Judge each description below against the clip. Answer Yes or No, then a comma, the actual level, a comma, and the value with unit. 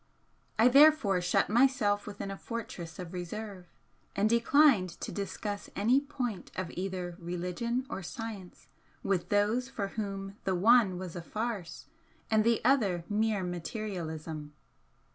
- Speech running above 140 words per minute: No, slow, 135 wpm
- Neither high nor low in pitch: No, high, 205 Hz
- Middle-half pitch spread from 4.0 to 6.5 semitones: Yes, average, 4.3 semitones